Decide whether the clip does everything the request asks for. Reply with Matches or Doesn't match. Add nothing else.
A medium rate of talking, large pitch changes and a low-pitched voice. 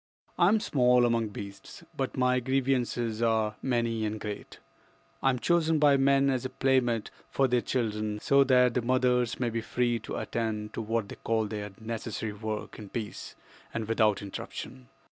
Doesn't match